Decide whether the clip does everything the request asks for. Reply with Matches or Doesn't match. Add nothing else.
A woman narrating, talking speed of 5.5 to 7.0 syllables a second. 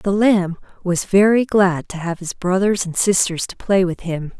Doesn't match